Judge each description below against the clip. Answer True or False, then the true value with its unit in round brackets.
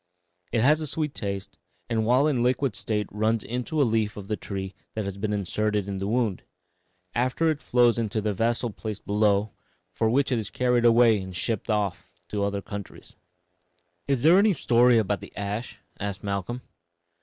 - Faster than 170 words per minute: True (190 wpm)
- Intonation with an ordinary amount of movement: True (3.4 semitones)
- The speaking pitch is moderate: False (110 Hz)